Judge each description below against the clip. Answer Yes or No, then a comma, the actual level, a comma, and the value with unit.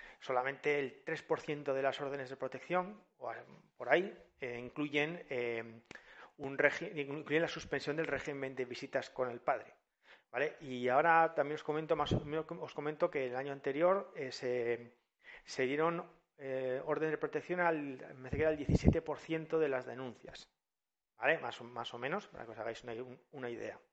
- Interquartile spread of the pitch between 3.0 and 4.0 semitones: Yes, average, 3.6 semitones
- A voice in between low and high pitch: Yes, medium, 145 Hz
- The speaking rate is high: No, average, 180 wpm